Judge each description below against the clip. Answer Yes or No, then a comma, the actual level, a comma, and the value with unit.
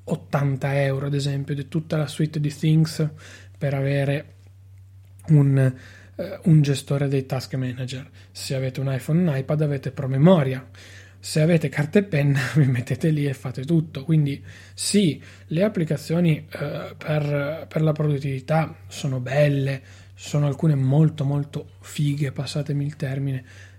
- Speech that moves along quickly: No, average, 145 wpm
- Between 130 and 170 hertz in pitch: Yes, medium, 140 Hz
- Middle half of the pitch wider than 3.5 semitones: No, average, 2.7 semitones